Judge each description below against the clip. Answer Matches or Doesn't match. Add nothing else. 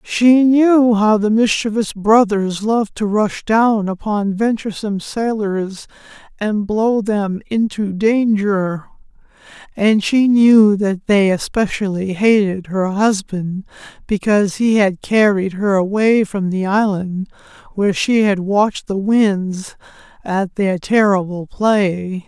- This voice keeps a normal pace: Doesn't match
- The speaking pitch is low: Doesn't match